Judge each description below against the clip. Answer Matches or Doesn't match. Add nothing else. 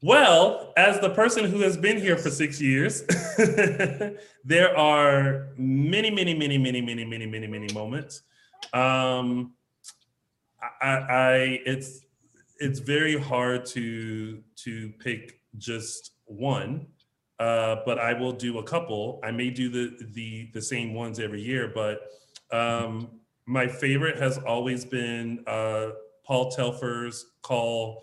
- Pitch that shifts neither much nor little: Matches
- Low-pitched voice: Matches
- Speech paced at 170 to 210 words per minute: Doesn't match